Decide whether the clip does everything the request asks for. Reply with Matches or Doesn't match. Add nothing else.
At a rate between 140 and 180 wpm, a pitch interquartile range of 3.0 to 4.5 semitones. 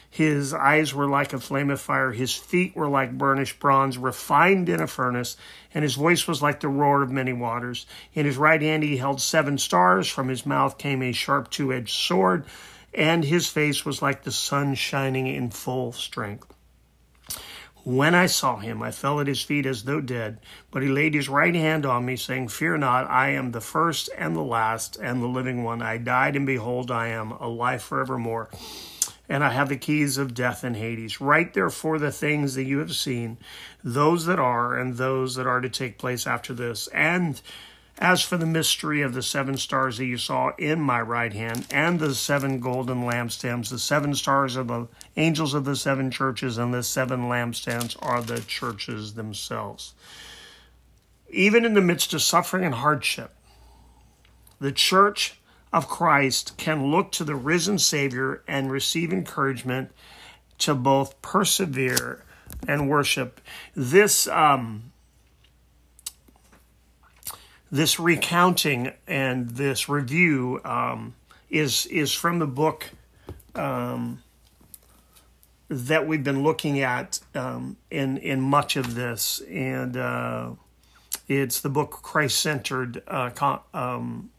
Matches